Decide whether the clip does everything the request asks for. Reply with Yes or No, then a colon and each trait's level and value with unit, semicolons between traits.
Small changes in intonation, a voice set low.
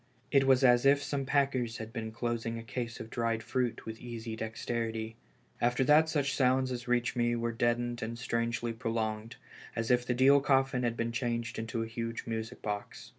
Yes: narrow, 1.8 semitones; low, 120 Hz